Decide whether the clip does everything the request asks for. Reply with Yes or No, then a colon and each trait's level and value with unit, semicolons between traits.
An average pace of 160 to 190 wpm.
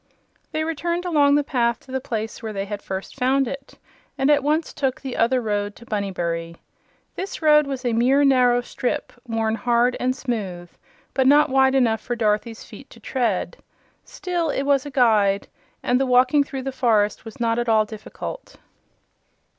Yes: average, 180 wpm